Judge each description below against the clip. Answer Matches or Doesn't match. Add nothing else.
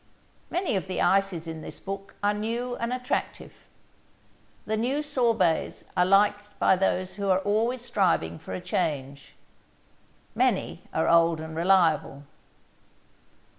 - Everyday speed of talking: Doesn't match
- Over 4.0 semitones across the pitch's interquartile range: Matches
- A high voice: Matches